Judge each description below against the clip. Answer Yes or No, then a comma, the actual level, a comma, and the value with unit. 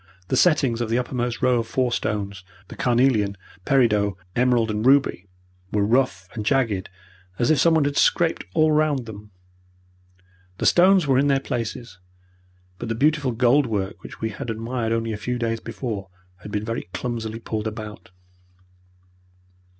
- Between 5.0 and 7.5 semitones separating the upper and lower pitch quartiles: No, average, 3.6 semitones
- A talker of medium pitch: No, low, 120 Hz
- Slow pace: No, average, 160 wpm